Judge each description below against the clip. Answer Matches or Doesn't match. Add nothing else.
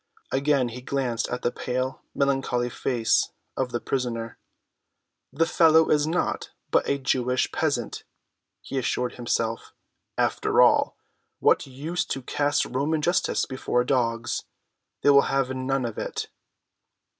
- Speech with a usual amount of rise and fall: Doesn't match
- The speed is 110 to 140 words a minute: Matches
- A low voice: Matches